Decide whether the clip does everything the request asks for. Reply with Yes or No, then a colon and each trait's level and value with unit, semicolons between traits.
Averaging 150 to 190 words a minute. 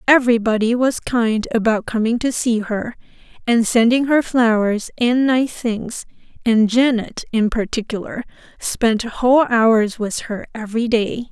No: average, 140 wpm